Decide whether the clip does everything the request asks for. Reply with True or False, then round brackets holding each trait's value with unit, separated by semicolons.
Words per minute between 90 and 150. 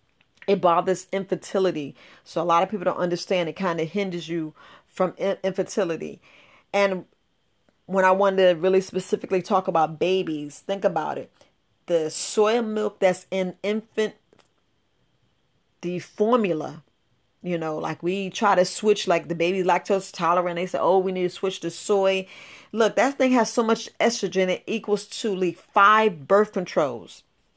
False (160 wpm)